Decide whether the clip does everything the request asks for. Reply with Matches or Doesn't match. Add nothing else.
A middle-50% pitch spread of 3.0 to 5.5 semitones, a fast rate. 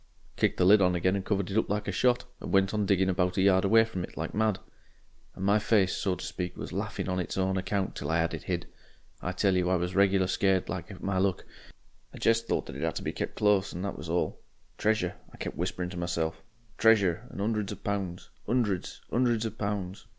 Doesn't match